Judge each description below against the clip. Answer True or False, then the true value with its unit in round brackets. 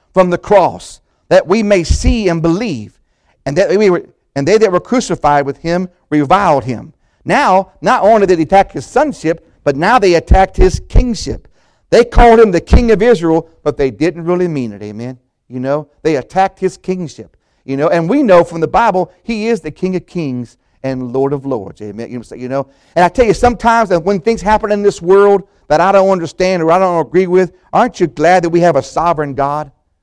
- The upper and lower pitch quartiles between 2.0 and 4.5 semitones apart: False (5.2 semitones)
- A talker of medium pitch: True (175 Hz)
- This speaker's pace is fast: True (210 wpm)